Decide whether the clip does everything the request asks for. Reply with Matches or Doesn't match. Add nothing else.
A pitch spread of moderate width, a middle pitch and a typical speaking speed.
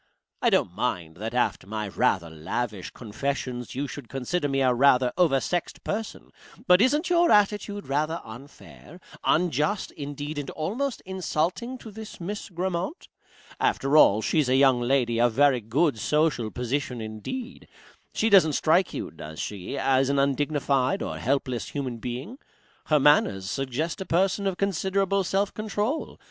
Doesn't match